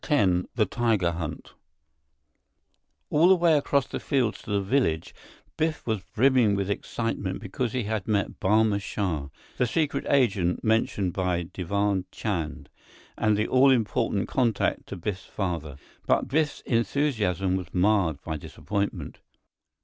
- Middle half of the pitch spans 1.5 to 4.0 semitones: No, average, 5.0 semitones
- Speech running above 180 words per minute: No, average, 140 wpm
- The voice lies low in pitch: Yes, low, 105 Hz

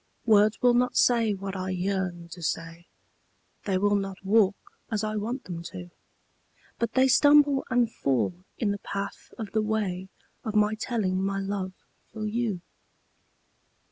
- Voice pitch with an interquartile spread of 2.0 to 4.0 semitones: Yes, average, 3.1 semitones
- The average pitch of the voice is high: Yes, high, 205 Hz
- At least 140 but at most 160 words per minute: Yes, average, 155 wpm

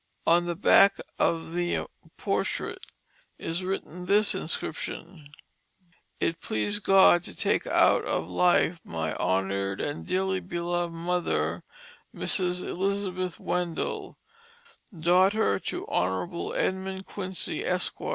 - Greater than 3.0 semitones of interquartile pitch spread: No, narrow, 2.5 semitones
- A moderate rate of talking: No, slow, 110 wpm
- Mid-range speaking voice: Yes, medium, 175 Hz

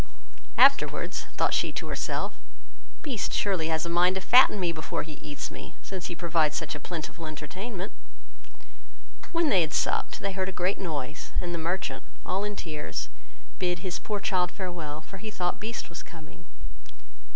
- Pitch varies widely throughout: No, average, 3.3 semitones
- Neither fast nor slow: Yes, average, 175 wpm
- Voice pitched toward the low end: No, medium, 175 Hz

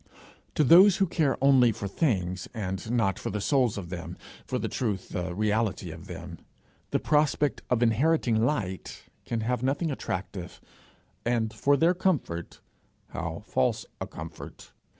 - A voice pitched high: No, low, 115 Hz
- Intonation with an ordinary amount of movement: No, wide, 6.7 semitones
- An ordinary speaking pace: Yes, average, 150 wpm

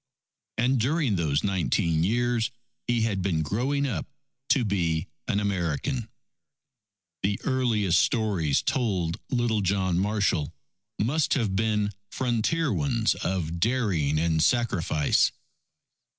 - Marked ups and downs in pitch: Yes, wide, 5.7 semitones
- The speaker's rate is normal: No, slow, 110 wpm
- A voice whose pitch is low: Yes, low, 105 Hz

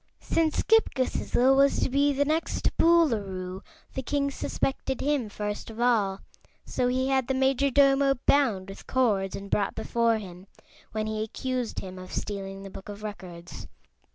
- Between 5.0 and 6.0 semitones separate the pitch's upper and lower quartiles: Yes, wide, 5.5 semitones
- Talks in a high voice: Yes, high, 240 Hz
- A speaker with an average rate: Yes, average, 160 wpm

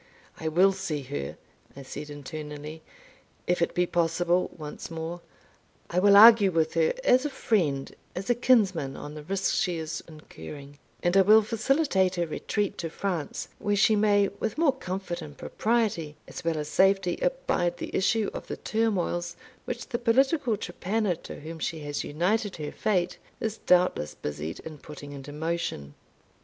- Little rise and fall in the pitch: No, average, 5.3 semitones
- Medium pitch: Yes, medium, 180 Hz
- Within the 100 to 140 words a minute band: No, average, 170 wpm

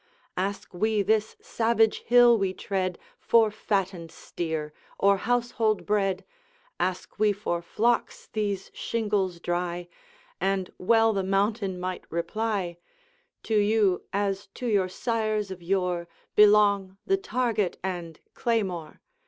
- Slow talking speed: Yes, slow, 120 wpm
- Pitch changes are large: No, average, 3.1 semitones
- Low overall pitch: No, high, 200 Hz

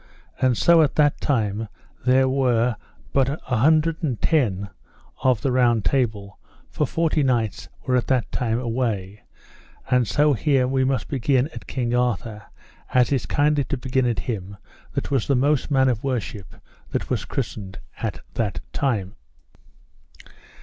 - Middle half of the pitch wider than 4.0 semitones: No, average, 3.4 semitones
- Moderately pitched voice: No, low, 125 Hz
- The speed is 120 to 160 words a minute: Yes, average, 150 wpm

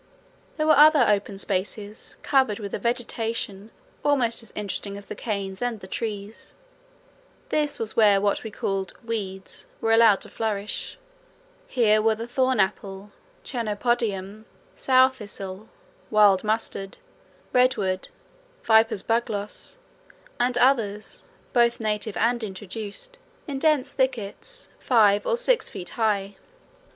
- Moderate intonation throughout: Yes, average, 3.3 semitones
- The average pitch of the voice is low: No, high, 220 Hz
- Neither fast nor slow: No, slow, 125 wpm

